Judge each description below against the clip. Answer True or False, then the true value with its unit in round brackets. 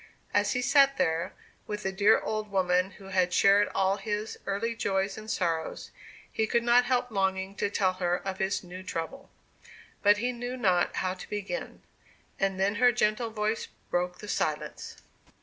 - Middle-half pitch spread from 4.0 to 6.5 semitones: False (2.8 semitones)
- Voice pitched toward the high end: True (200 Hz)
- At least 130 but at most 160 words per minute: False (175 wpm)